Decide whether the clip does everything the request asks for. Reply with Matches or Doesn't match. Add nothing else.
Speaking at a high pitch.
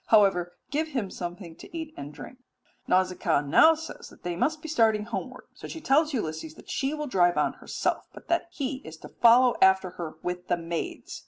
Matches